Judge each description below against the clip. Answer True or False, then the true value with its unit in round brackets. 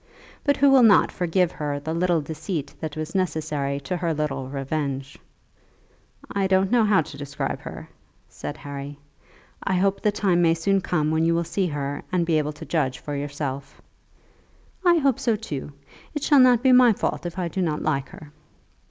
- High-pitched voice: False (165 Hz)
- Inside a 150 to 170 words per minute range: False (190 wpm)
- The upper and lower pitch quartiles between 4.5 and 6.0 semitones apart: True (5.0 semitones)